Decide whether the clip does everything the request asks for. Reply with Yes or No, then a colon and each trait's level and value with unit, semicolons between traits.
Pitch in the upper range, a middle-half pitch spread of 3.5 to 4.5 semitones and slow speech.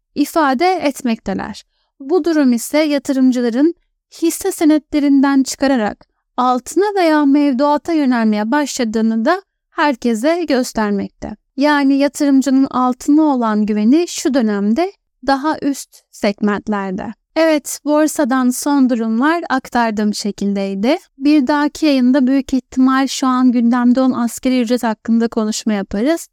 No: very high, 270 Hz; average, 4.0 semitones; average, 105 wpm